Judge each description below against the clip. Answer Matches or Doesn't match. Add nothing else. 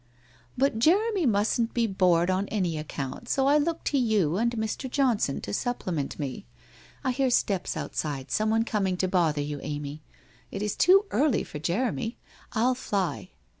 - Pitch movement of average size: Doesn't match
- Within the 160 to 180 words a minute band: Matches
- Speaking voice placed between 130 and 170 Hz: Doesn't match